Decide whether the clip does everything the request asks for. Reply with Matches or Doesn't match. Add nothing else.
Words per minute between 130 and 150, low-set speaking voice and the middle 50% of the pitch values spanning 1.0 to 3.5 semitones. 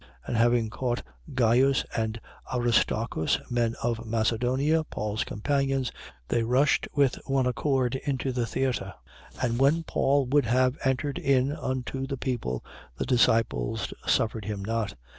Matches